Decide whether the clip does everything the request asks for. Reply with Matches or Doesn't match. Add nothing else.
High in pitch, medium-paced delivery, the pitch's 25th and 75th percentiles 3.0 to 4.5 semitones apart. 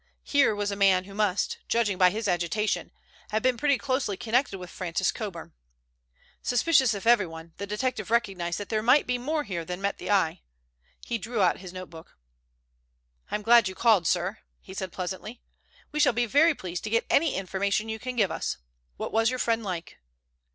Matches